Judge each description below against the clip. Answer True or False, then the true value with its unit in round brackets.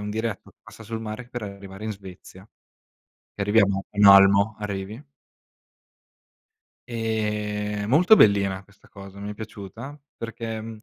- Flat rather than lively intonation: True (2.1 semitones)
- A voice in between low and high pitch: False (105 Hz)